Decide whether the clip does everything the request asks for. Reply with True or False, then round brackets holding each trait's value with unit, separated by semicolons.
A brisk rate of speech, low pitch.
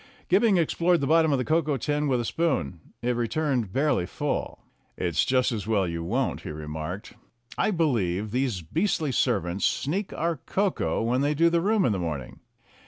False (180 wpm; 130 Hz)